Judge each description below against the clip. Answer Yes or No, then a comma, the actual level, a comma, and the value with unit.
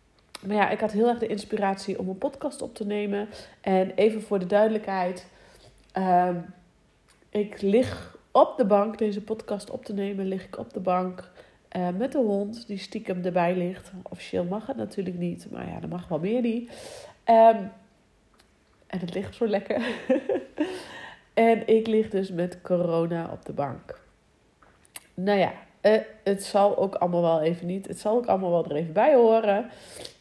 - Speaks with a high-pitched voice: Yes, high, 200 Hz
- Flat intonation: No, average, 3.3 semitones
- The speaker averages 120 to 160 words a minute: No, average, 175 wpm